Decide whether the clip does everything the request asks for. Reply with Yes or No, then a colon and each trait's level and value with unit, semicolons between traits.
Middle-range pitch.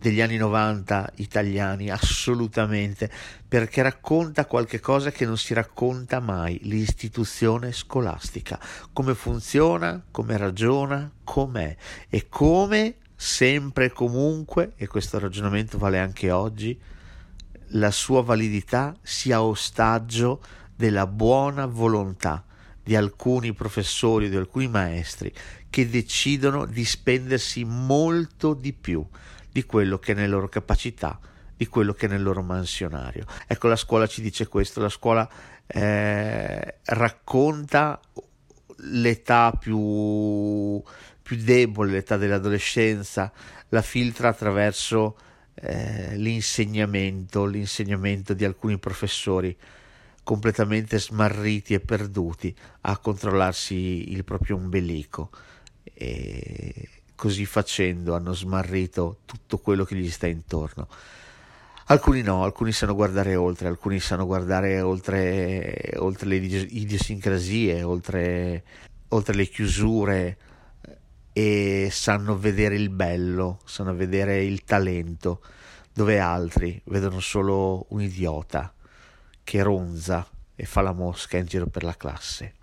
No: low, 105 Hz